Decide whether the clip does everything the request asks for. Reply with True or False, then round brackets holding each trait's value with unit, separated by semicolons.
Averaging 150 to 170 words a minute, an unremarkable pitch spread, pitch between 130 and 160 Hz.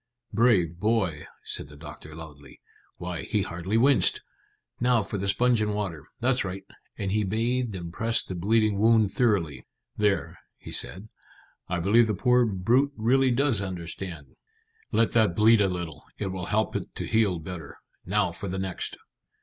False (165 wpm; 4.3 semitones; 100 Hz)